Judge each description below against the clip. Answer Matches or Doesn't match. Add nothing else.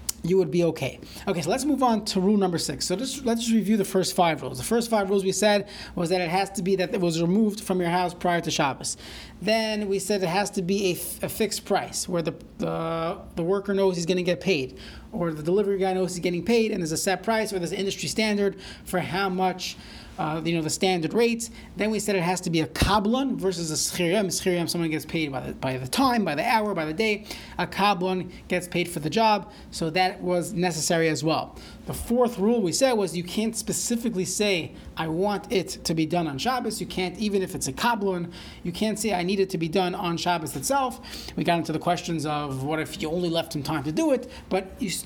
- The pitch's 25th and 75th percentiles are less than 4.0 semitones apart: Matches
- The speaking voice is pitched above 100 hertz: Matches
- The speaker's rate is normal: Doesn't match